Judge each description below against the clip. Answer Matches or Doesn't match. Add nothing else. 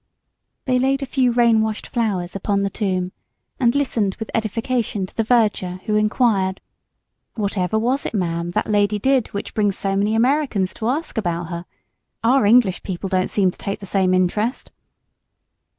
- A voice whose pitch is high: Matches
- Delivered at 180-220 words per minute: Doesn't match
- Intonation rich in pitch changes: Doesn't match